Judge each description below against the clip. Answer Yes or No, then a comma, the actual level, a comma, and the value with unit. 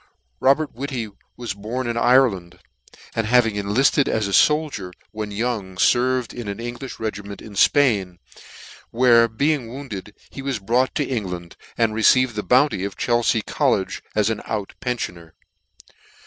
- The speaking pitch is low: Yes, low, 115 Hz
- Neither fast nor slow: Yes, average, 150 wpm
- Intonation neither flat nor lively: Yes, average, 3.9 semitones